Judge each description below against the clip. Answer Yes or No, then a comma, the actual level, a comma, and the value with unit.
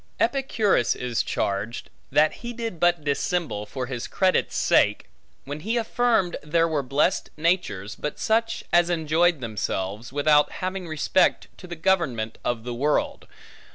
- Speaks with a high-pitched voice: No, medium, 155 Hz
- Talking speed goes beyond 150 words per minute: No, average, 145 wpm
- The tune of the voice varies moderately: No, wide, 6.8 semitones